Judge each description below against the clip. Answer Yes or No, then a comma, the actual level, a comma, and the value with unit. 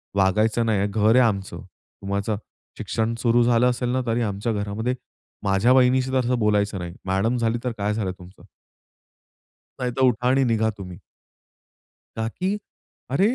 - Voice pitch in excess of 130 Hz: No, low, 110 Hz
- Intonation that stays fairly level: No, average, 3.5 semitones